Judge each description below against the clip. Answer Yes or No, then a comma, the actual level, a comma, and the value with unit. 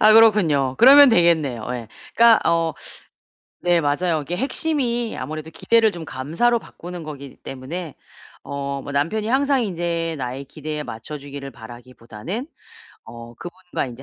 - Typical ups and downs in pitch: No, wide, 7.6 semitones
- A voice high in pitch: No, medium, 160 Hz